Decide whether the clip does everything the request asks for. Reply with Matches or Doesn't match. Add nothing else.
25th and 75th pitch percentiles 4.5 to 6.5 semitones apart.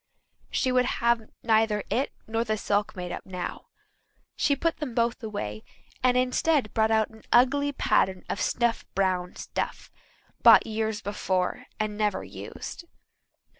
Doesn't match